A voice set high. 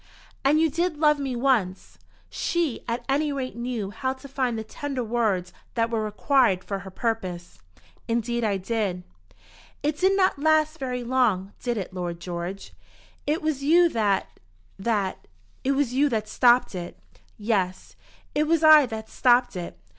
Yes: high, 240 Hz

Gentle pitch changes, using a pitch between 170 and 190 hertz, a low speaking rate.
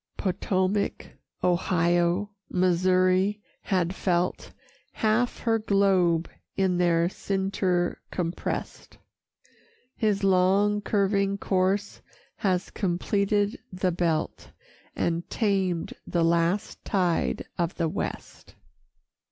Yes: narrow, 2.3 semitones; medium, 185 Hz; slow, 85 wpm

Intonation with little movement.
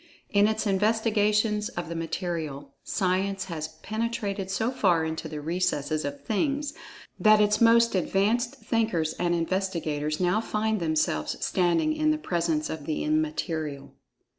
No: average, 5.2 semitones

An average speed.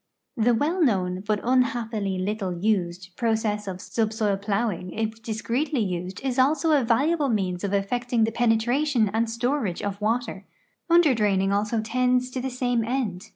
Yes: average, 155 wpm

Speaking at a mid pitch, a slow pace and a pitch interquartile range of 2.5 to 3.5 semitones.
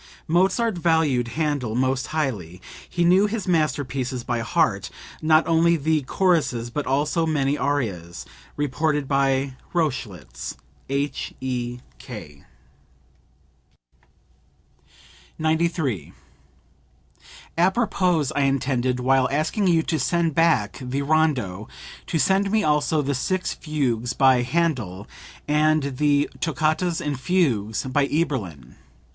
No: medium, 145 Hz; slow, 105 wpm; average, 4.4 semitones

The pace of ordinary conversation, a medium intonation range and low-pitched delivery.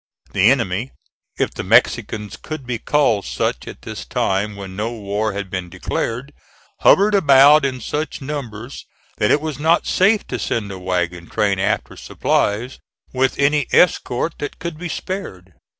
No: average, 160 wpm; wide, 6.6 semitones; low, 120 Hz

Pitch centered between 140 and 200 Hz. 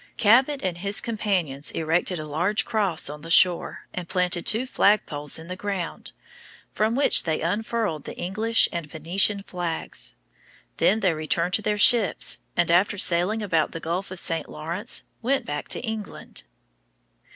Yes: medium, 185 Hz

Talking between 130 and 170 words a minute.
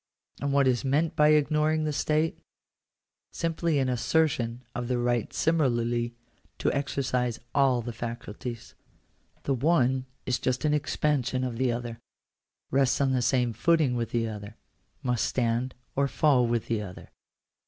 Yes: average, 155 wpm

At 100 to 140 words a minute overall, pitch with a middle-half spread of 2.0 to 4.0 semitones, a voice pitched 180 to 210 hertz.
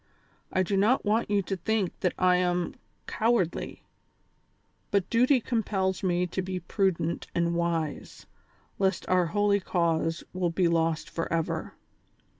Yes: slow, 135 wpm; average, 3.0 semitones; medium, 185 Hz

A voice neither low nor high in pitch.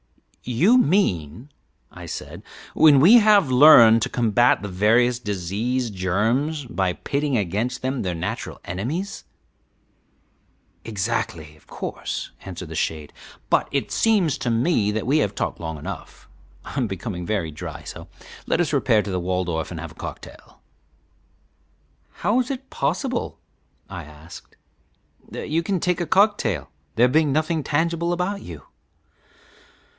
No: low, 120 Hz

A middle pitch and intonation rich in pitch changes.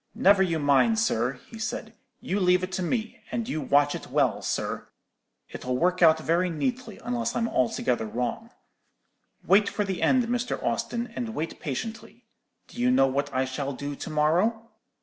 Yes: medium, 180 Hz; wide, 8.0 semitones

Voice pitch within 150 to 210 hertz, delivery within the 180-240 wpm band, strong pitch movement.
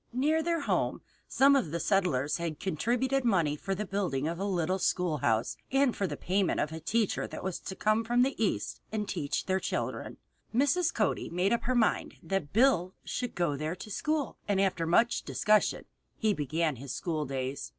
Yes: high, 190 Hz; average, 190 wpm; wide, 6.5 semitones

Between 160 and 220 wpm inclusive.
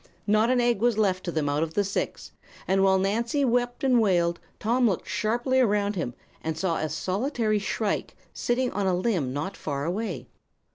Yes: average, 190 wpm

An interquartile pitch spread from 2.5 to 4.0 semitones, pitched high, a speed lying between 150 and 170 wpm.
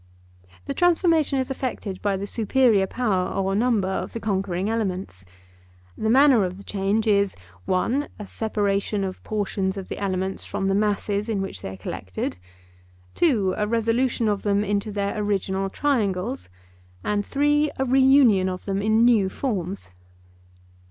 Yes: average, 3.4 semitones; high, 205 Hz; average, 155 wpm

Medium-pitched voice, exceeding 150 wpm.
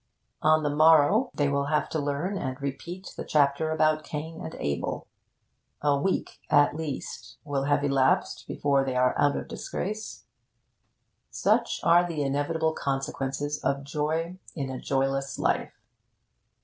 No: medium, 145 Hz; average, 145 wpm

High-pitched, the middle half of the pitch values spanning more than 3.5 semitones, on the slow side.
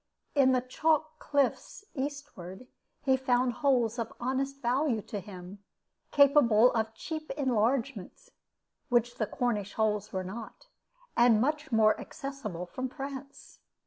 Yes: very high, 250 Hz; average, 4.1 semitones; slow, 125 wpm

